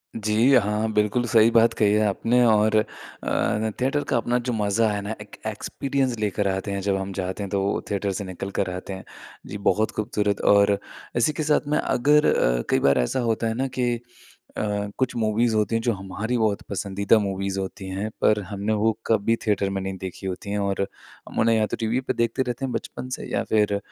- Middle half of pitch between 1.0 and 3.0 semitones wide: Yes, narrow, 2.6 semitones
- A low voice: Yes, low, 105 Hz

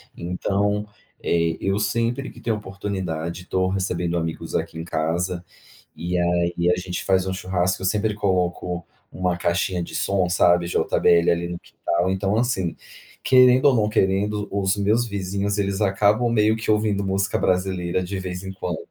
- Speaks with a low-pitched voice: Yes, very low, 95 Hz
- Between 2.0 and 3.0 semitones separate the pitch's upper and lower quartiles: Yes, average, 2.7 semitones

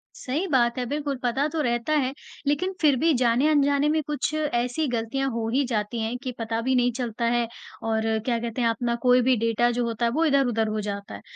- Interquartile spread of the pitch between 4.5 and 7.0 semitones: No, average, 3.4 semitones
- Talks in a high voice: Yes, high, 245 Hz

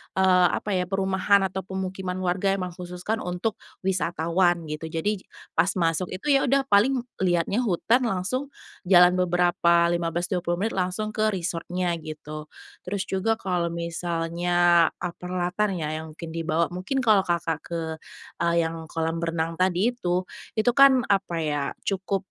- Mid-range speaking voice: Yes, medium, 180 Hz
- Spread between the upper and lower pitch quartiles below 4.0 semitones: Yes, narrow, 2.4 semitones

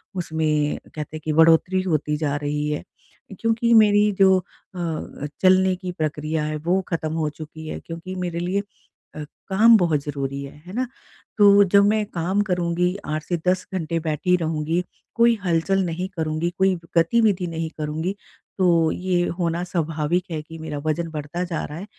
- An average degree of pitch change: Yes, average, 3.3 semitones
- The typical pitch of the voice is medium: Yes, medium, 170 Hz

